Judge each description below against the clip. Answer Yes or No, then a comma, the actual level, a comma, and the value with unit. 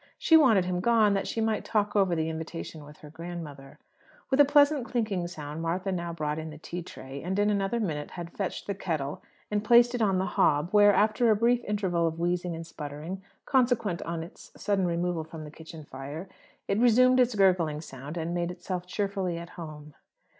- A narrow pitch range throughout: No, average, 4.4 semitones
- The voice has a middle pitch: Yes, medium, 180 Hz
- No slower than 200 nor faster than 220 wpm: Yes, fast, 205 wpm